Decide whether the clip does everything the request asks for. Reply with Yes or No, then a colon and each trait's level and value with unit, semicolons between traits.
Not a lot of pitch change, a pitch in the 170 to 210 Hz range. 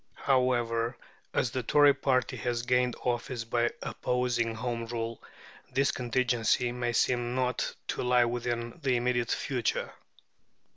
No: narrow, 1.2 semitones; low, 120 Hz